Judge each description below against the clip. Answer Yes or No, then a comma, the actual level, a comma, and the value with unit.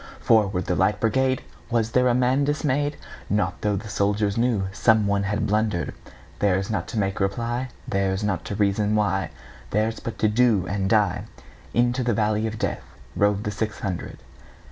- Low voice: Yes, low, 105 Hz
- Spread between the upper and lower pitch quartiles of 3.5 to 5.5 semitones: No, average, 2.8 semitones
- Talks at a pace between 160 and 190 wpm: No, average, 145 wpm